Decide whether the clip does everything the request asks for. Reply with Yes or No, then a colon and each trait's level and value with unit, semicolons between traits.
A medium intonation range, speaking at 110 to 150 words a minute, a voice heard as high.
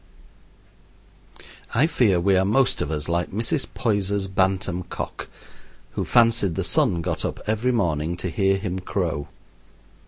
No: average, 3.8 semitones; average, 145 wpm; very low, 95 Hz